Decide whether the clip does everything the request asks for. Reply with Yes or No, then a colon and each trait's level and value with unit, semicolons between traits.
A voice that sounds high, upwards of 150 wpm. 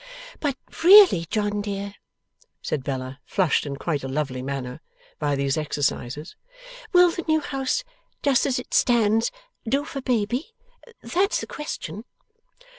No: high, 205 Hz; slow, 135 wpm